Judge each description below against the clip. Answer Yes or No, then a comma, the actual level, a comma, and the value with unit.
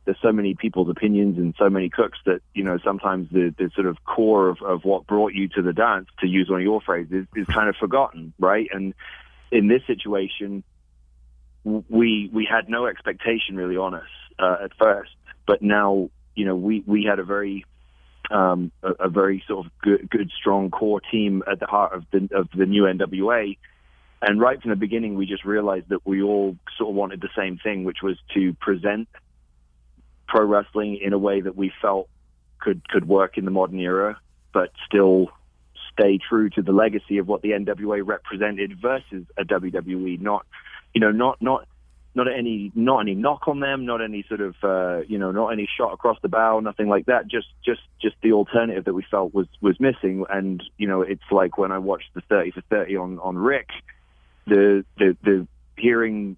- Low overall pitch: Yes, low, 100 Hz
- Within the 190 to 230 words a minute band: Yes, fast, 205 wpm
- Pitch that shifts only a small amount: Yes, narrow, 2.1 semitones